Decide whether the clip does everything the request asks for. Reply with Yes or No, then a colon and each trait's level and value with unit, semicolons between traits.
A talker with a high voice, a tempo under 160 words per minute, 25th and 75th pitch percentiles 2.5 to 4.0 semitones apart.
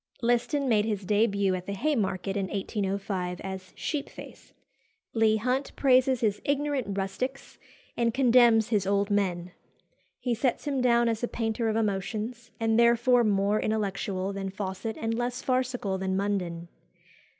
Yes: high, 220 Hz; average, 145 wpm; average, 3.7 semitones